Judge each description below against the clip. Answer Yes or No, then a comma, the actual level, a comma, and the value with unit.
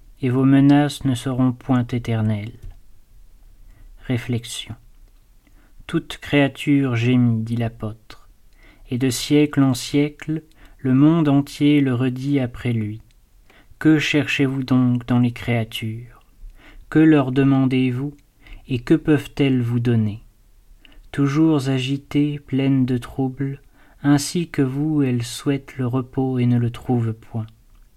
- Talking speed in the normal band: No, slow, 125 wpm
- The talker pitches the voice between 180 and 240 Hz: No, low, 130 Hz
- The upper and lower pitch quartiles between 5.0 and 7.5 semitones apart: No, average, 3.6 semitones